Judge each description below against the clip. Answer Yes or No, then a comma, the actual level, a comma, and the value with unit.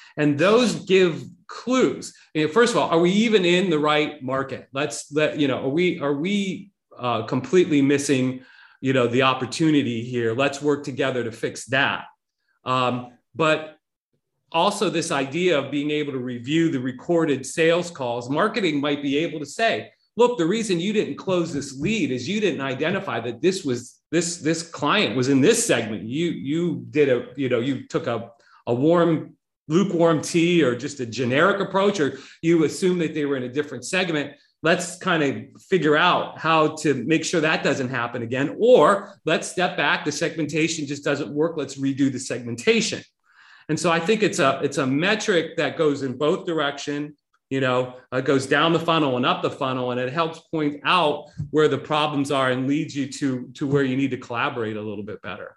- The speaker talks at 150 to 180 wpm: No, average, 195 wpm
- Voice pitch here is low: No, medium, 150 Hz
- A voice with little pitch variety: No, average, 3.8 semitones